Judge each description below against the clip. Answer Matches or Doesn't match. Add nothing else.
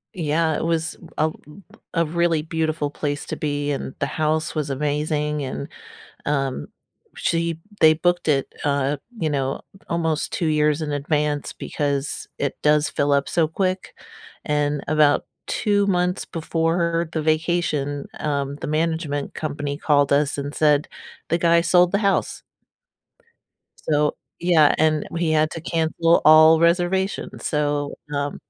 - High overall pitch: Doesn't match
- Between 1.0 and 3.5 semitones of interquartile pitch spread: Matches